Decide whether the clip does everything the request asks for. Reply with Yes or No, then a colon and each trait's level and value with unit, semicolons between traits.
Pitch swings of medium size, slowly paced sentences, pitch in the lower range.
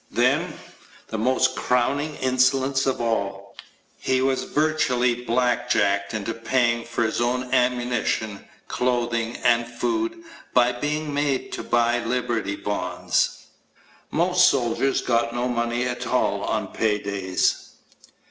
No: narrow, 2.1 semitones; slow, 120 wpm; low, 120 Hz